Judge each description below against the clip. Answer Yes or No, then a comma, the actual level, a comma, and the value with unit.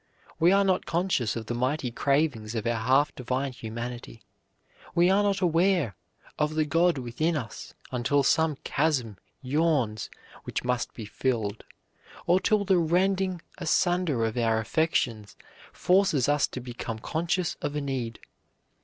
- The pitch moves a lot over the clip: Yes, wide, 6.3 semitones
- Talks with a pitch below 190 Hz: Yes, medium, 140 Hz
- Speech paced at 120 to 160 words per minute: Yes, average, 145 wpm